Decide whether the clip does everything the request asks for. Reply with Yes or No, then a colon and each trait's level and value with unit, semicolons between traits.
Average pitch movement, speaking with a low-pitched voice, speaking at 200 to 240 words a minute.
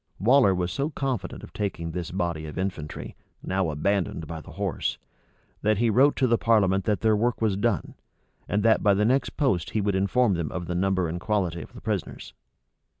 Yes: average, 4.2 semitones; low, 100 Hz; fast, 205 wpm